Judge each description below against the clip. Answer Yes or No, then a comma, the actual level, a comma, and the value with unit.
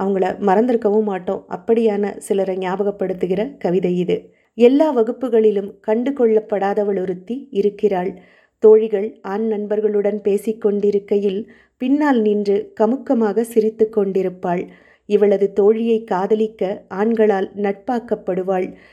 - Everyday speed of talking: Yes, average, 90 wpm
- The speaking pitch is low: No, high, 210 Hz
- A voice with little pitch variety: Yes, narrow, 1.9 semitones